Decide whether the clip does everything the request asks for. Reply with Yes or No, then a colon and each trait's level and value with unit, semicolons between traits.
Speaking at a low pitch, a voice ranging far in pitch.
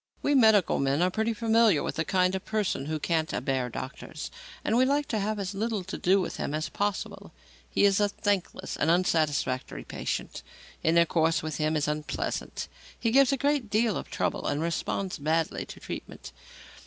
No: medium, 185 Hz; wide, 5.7 semitones